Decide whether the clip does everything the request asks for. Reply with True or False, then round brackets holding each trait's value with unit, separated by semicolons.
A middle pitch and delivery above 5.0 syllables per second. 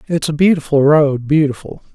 True (150 Hz; 5.2 syllables/s)